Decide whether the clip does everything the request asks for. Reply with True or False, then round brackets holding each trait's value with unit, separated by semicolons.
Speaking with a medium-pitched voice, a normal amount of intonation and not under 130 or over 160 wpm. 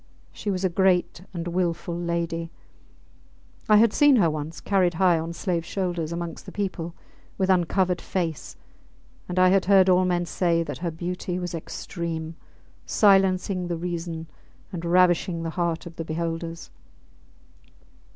False (175 Hz; 1.8 semitones; 150 wpm)